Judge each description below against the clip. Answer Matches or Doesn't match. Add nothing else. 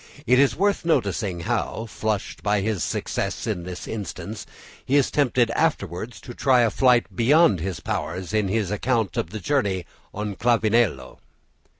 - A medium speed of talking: Matches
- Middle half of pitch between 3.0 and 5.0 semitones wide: Matches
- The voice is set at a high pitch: Doesn't match